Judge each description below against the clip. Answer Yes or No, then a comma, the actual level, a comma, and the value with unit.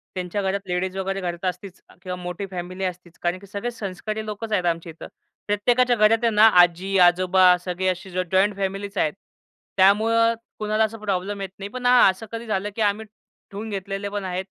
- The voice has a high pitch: Yes, high, 195 Hz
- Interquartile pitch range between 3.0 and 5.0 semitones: No, narrow, 2.5 semitones